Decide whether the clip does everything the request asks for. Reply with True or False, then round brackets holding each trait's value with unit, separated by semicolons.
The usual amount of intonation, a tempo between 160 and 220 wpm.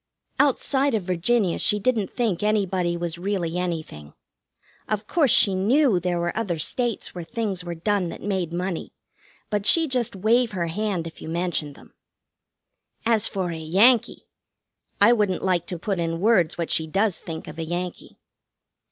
True (4.1 semitones; 170 wpm)